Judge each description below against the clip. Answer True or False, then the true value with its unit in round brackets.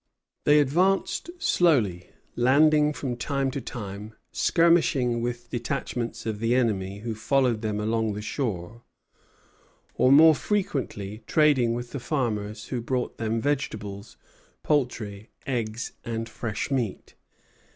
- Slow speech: True (120 wpm)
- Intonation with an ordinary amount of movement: True (4.3 semitones)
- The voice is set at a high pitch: False (120 Hz)